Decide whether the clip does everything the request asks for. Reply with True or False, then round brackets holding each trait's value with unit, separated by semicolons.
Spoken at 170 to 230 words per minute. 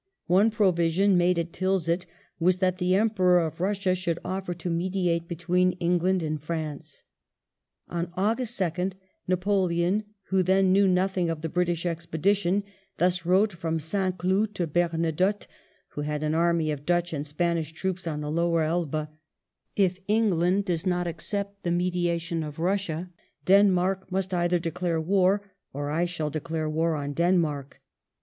False (160 wpm)